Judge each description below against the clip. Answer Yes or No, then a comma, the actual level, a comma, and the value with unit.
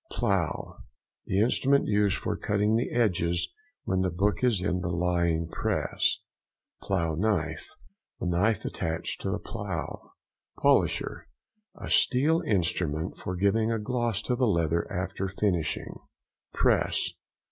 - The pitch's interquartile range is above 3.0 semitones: Yes, average, 4.3 semitones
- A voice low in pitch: Yes, very low, 95 Hz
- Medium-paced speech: No, slow, 125 wpm